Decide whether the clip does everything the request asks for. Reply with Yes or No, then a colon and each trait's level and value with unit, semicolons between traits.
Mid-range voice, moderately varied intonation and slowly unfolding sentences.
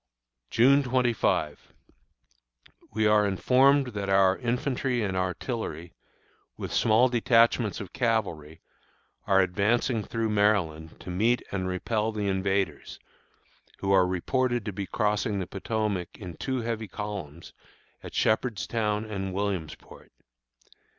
No: low, 105 Hz; average, 3.6 semitones; slow, 115 wpm